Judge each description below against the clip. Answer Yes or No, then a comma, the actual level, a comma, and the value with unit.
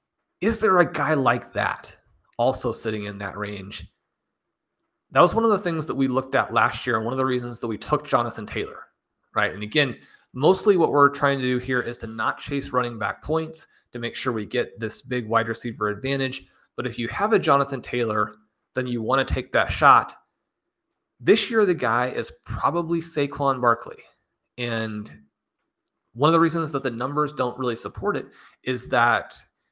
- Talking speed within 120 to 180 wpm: No, average, 195 wpm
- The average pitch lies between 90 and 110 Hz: No, low, 125 Hz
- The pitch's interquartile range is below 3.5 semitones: No, average, 4.1 semitones